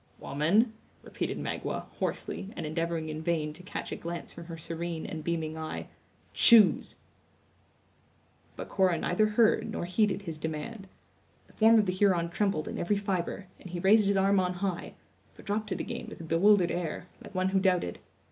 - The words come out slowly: No, average, 180 wpm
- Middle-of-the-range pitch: Yes, medium, 180 Hz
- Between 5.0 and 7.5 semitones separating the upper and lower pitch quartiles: No, average, 3.4 semitones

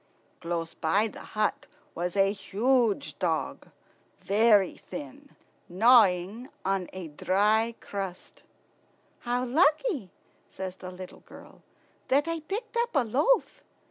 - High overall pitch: Yes, high, 215 Hz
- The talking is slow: Yes, slow, 110 wpm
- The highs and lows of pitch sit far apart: Yes, wide, 6.2 semitones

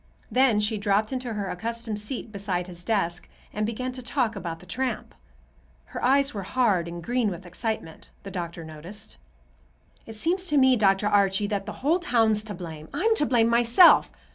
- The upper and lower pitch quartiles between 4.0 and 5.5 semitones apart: Yes, average, 4.4 semitones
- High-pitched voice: Yes, high, 215 Hz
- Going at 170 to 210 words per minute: Yes, average, 185 wpm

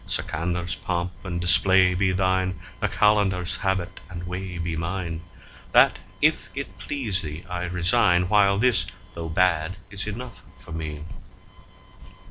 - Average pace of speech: No, slow, 130 wpm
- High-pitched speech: No, very low, 90 Hz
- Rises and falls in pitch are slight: Yes, narrow, 1.8 semitones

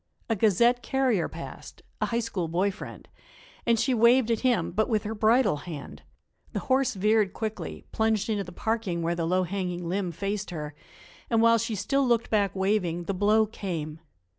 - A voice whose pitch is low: No, high, 210 Hz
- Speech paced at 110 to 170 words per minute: No, average, 185 wpm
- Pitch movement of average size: Yes, average, 4.2 semitones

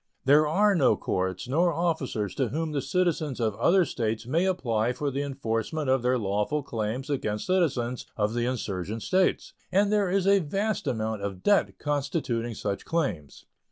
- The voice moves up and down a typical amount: No, wide, 7.0 semitones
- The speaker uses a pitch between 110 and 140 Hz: Yes, low, 135 Hz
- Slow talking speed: No, average, 170 wpm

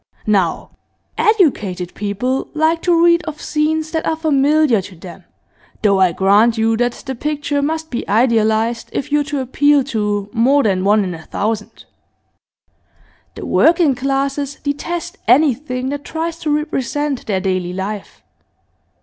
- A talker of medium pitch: No, very high, 265 Hz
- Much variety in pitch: Yes, wide, 6.4 semitones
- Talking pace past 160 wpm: No, average, 145 wpm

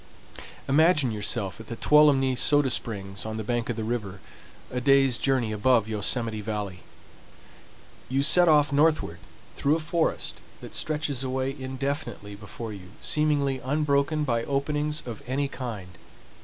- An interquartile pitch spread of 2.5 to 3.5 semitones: No, average, 4.8 semitones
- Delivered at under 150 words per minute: Yes, average, 140 wpm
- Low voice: Yes, low, 130 Hz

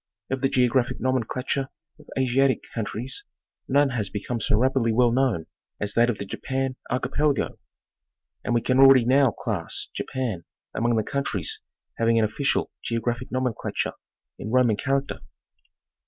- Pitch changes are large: No, average, 2.7 semitones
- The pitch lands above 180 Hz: No, low, 125 Hz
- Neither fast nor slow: Yes, average, 145 wpm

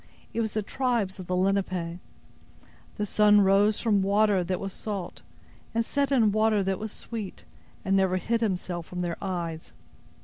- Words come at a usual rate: Yes, average, 170 wpm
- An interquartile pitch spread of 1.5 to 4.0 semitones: Yes, average, 2.8 semitones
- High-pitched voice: Yes, high, 195 Hz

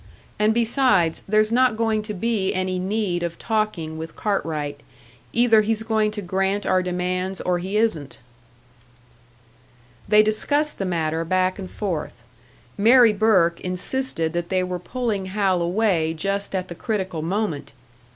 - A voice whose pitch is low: No, high, 190 Hz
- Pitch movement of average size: Yes, average, 3.7 semitones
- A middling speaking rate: Yes, average, 145 wpm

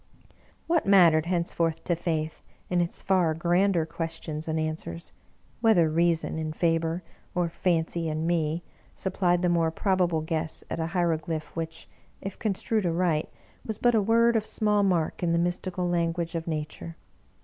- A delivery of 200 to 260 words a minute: No, average, 160 wpm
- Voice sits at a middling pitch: Yes, medium, 170 Hz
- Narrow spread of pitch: Yes, narrow, 2.2 semitones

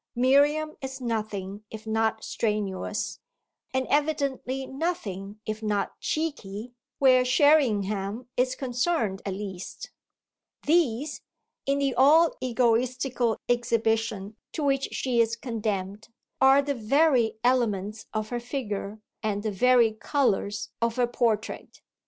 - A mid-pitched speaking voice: No, high, 235 Hz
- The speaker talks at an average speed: No, slow, 115 wpm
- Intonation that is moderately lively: Yes, average, 4.0 semitones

